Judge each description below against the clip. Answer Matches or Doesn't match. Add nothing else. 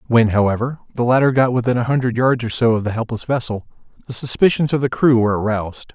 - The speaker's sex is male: Matches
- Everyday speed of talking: Doesn't match